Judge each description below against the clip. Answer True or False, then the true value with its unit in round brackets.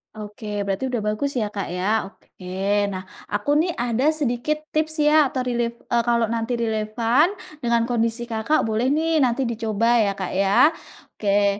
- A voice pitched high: True (230 Hz)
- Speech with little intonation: False (3.8 semitones)